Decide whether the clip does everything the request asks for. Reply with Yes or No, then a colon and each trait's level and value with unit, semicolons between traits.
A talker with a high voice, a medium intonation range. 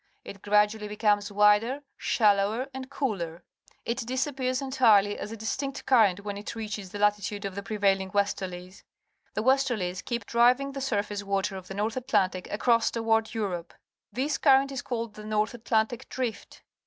Yes: high, 215 Hz; average, 3.5 semitones